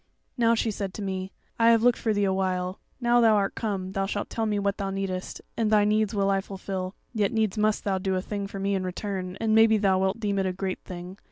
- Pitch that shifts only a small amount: Yes, narrow, 2.2 semitones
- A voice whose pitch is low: No, high, 200 Hz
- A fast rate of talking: Yes, fast, 260 wpm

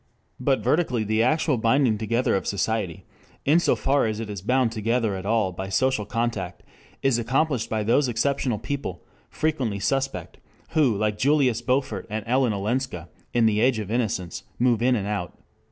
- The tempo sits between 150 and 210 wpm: Yes, average, 170 wpm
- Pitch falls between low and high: No, low, 115 Hz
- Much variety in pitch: No, average, 3.8 semitones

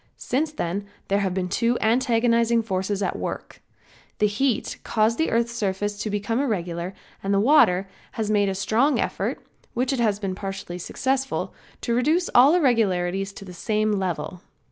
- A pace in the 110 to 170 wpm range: Yes, average, 165 wpm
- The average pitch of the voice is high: Yes, high, 210 Hz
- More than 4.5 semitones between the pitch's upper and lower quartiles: No, average, 3.7 semitones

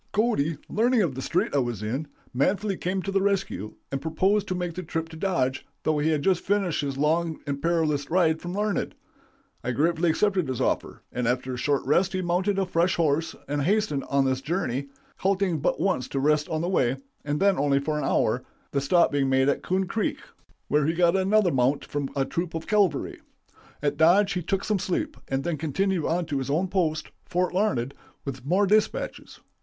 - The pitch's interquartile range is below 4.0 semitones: No, average, 5.1 semitones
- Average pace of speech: No, fast, 210 wpm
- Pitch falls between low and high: Yes, medium, 165 Hz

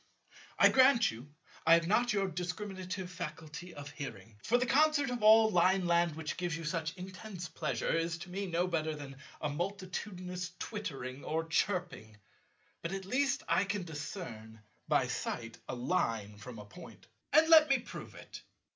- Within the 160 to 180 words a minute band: Yes, average, 165 wpm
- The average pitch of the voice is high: No, medium, 175 Hz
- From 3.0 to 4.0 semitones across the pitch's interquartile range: No, average, 4.8 semitones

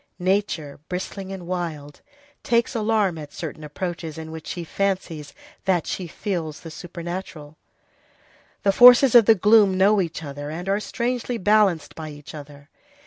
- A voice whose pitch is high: No, medium, 180 Hz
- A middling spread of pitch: Yes, average, 4.5 semitones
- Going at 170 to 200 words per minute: No, average, 150 wpm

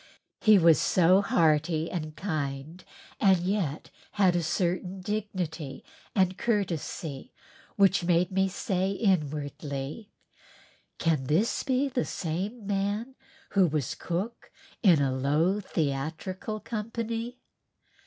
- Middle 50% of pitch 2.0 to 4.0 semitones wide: No, average, 4.6 semitones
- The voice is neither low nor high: Yes, medium, 180 Hz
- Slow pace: Yes, slow, 110 wpm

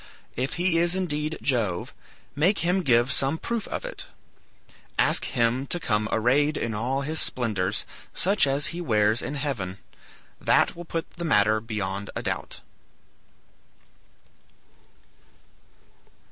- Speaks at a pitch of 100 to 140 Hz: Yes, low, 135 Hz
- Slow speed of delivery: Yes, slow, 130 wpm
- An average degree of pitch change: No, wide, 7.1 semitones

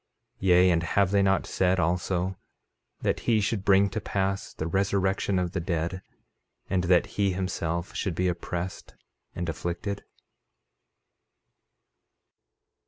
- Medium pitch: No, very low, 95 Hz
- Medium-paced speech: No, slow, 130 wpm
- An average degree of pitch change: No, narrow, 1.9 semitones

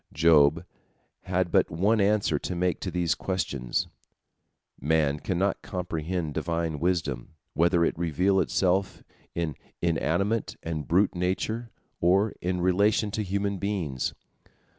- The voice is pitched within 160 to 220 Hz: No, very low, 90 Hz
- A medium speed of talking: No, slow, 120 wpm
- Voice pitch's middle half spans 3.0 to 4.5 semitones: Yes, average, 3.3 semitones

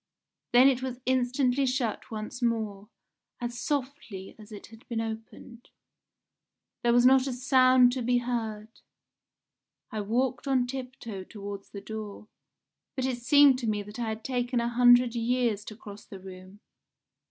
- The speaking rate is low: No, average, 155 wpm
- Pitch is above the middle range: Yes, high, 240 Hz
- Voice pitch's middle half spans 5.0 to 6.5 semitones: No, average, 2.9 semitones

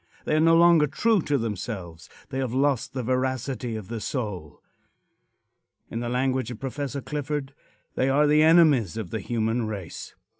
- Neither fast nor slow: Yes, average, 165 wpm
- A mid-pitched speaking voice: No, low, 130 Hz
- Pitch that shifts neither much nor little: Yes, average, 4.5 semitones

